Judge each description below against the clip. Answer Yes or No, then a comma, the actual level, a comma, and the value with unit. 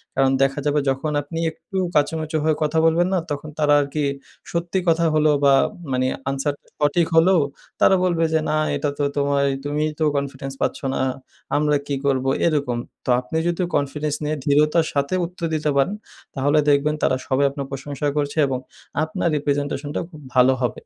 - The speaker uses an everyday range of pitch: No, narrow, 2.1 semitones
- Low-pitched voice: No, medium, 145 Hz